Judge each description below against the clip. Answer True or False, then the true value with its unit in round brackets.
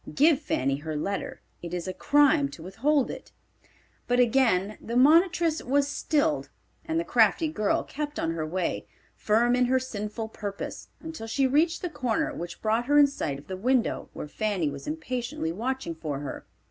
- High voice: True (245 Hz)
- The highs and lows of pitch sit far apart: True (7.4 semitones)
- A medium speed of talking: True (180 wpm)